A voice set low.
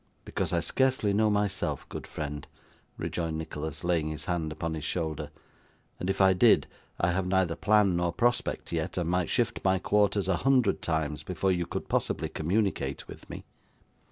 Yes: very low, 90 Hz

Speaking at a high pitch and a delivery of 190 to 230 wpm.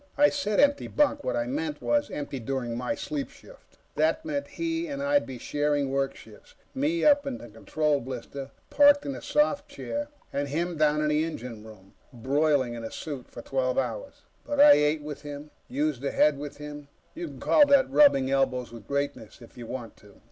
No: medium, 150 Hz; fast, 205 wpm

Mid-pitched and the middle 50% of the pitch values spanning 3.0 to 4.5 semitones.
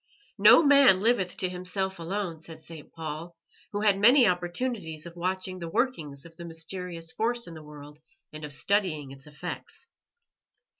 Yes: medium, 175 Hz; average, 3.8 semitones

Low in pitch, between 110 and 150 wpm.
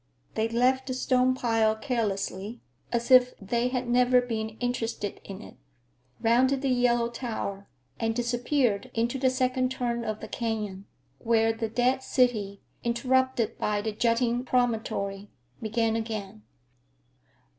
No: high, 235 Hz; slow, 135 wpm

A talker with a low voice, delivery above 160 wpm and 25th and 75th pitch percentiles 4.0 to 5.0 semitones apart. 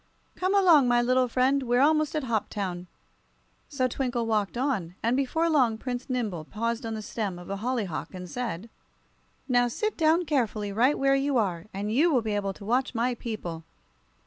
No: high, 240 Hz; average, 185 wpm; average, 4.4 semitones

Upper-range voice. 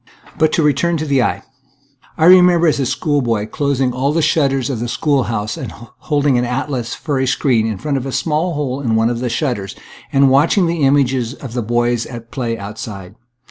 No: low, 135 Hz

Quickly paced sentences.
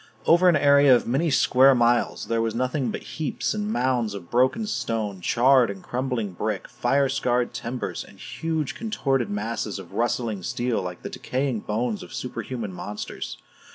No: average, 165 wpm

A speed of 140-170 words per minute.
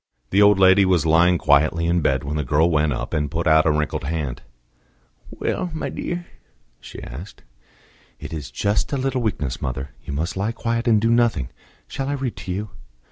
No: average, 195 wpm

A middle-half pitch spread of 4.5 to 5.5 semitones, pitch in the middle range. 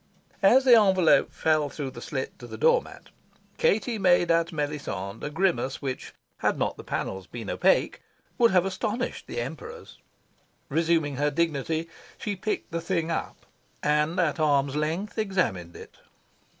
Yes: average, 5.0 semitones; medium, 160 Hz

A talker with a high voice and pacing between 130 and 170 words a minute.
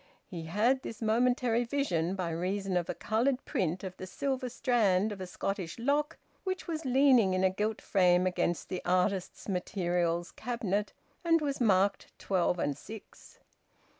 Yes: high, 200 Hz; average, 160 wpm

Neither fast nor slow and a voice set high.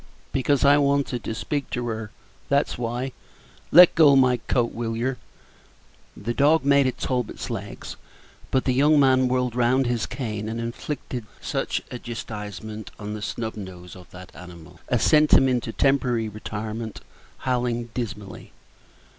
No: average, 155 wpm; low, 120 Hz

